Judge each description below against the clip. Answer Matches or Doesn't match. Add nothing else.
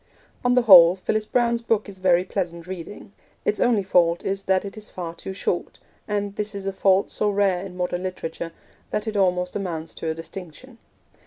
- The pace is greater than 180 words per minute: Matches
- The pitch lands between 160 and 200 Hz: Matches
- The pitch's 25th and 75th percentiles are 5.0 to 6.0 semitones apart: Doesn't match